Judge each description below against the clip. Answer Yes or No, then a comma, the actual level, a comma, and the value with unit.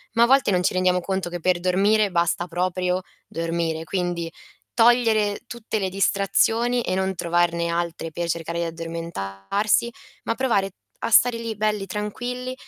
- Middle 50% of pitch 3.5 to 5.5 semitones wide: Yes, average, 4.2 semitones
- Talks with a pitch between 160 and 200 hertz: Yes, medium, 185 Hz